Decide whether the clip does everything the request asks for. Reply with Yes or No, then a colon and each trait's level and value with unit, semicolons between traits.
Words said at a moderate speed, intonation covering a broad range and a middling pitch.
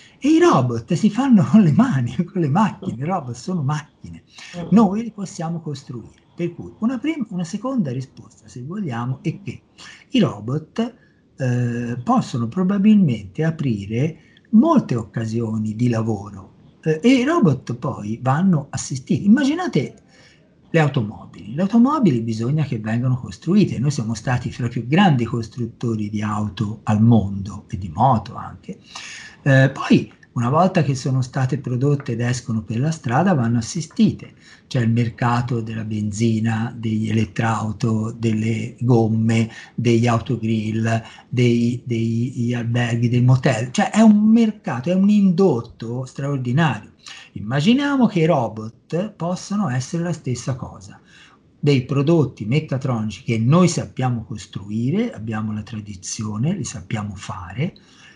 No: average, 140 wpm; wide, 7.0 semitones; low, 125 Hz